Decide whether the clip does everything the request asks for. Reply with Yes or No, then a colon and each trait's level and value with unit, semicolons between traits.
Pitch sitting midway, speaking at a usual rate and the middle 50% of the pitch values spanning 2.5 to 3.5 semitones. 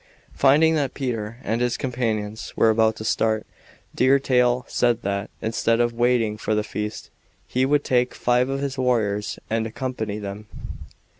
No: low, 120 Hz; average, 160 wpm; average, 2.8 semitones